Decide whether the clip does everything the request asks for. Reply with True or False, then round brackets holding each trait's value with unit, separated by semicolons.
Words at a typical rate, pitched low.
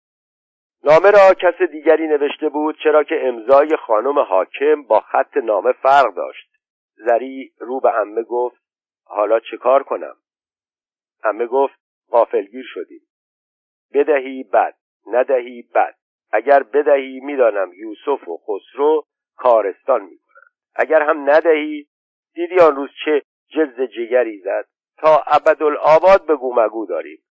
False (125 wpm; 155 Hz)